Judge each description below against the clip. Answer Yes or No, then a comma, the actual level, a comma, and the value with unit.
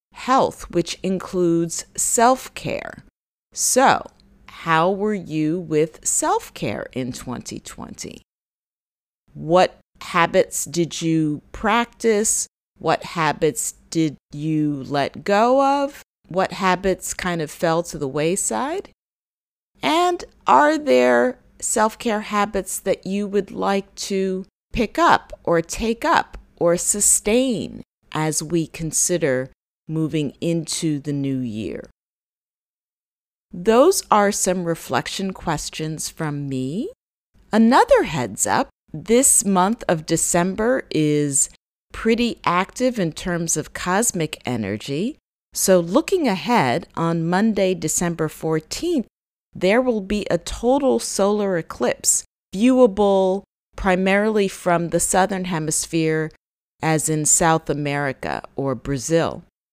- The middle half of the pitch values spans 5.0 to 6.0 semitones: Yes, average, 5.3 semitones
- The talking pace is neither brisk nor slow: No, slow, 105 wpm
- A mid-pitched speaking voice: Yes, medium, 180 Hz